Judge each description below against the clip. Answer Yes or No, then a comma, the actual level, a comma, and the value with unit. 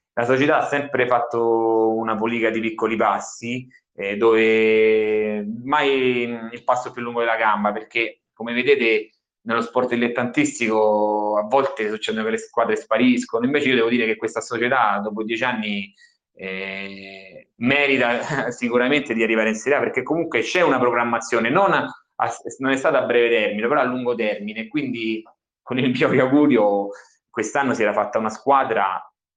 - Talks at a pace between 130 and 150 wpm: No, average, 160 wpm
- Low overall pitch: Yes, low, 115 Hz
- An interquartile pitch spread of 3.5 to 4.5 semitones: No, average, 2.9 semitones